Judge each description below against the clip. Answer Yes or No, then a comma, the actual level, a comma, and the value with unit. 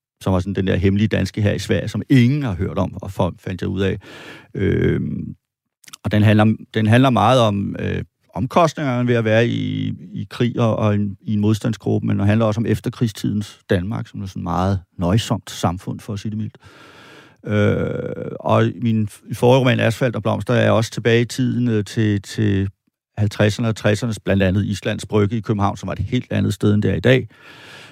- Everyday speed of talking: Yes, average, 210 wpm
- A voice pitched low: Yes, low, 110 Hz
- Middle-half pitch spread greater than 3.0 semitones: No, average, 2.7 semitones